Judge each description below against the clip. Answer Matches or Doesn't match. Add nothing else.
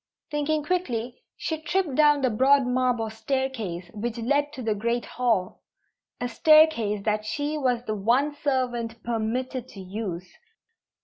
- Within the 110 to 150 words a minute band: Matches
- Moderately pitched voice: Doesn't match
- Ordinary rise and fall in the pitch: Matches